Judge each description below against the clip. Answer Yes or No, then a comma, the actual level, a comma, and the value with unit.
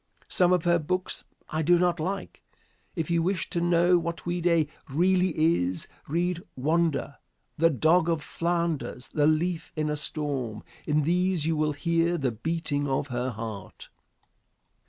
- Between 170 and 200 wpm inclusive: No, average, 155 wpm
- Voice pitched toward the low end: No, medium, 165 Hz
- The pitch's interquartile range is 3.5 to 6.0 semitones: No, average, 2.9 semitones